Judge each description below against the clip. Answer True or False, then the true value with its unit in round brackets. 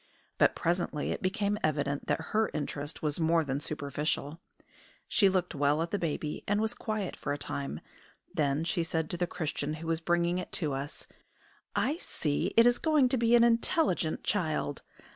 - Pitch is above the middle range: False (165 Hz)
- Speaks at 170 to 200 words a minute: True (180 wpm)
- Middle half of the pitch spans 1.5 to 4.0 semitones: False (5.4 semitones)